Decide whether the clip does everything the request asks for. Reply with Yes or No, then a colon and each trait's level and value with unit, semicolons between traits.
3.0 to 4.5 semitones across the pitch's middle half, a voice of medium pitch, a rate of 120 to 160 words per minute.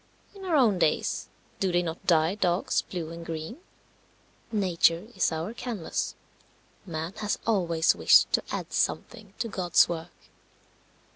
Yes: average, 4.2 semitones; medium, 175 Hz; average, 140 wpm